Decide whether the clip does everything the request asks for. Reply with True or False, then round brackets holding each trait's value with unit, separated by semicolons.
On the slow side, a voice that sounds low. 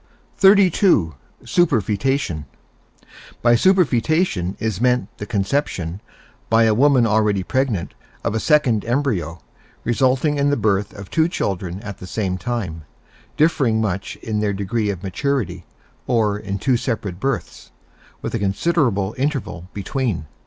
True (130 wpm; 110 Hz)